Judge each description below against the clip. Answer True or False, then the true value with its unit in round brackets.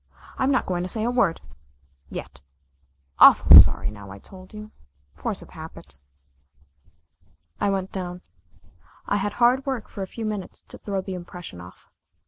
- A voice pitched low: False (190 Hz)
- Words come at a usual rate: True (160 wpm)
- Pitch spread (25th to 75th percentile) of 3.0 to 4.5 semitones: True (3.3 semitones)